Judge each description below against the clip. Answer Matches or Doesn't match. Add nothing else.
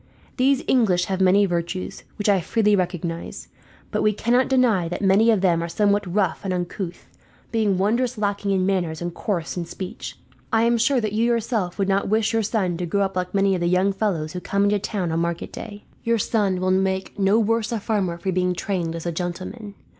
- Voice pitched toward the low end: Doesn't match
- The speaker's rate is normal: Doesn't match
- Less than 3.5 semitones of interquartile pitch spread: Matches